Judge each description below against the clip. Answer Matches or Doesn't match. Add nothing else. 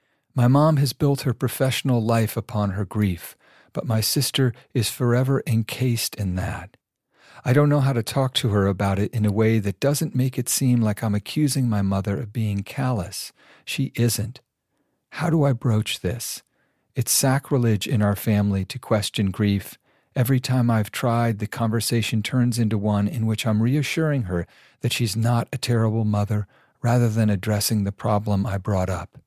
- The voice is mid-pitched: Doesn't match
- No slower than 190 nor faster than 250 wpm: Doesn't match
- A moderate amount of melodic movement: Matches